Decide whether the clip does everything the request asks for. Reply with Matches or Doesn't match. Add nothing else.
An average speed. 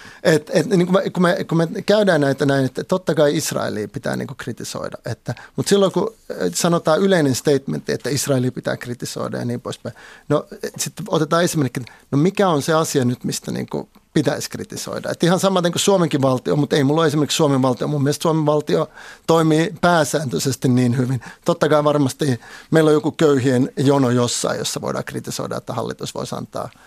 Doesn't match